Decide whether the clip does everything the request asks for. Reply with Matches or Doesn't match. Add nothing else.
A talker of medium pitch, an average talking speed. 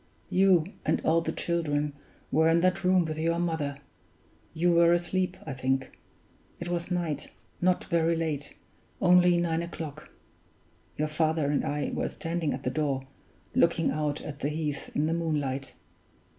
Matches